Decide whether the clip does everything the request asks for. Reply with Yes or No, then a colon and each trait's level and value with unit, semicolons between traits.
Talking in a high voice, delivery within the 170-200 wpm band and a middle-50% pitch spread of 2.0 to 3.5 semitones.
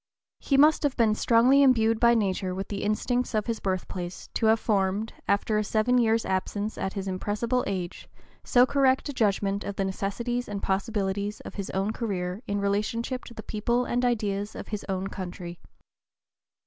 Yes: high, 210 Hz; average, 180 wpm; average, 3.2 semitones